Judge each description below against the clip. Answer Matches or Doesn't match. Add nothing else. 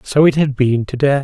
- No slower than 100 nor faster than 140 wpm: Doesn't match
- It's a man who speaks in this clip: Matches